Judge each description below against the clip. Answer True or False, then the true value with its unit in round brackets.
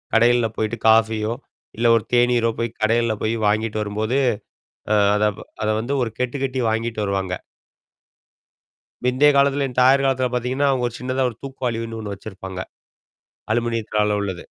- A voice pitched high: False (115 Hz)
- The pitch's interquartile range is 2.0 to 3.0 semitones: True (2.6 semitones)